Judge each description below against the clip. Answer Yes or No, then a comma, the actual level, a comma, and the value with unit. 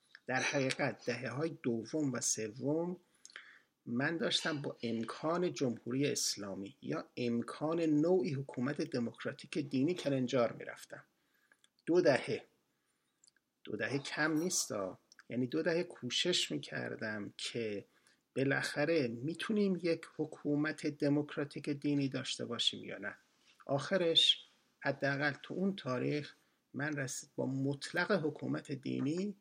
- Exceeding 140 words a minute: No, average, 110 wpm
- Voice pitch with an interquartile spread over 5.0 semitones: No, average, 3.9 semitones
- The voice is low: No, medium, 145 Hz